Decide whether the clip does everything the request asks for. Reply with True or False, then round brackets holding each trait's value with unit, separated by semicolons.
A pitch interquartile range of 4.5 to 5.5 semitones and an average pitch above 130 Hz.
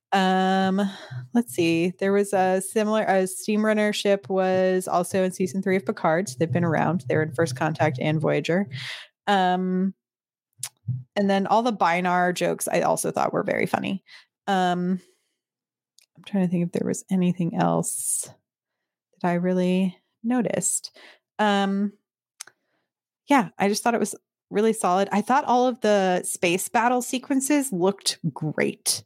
False (2.8 semitones; 190 Hz)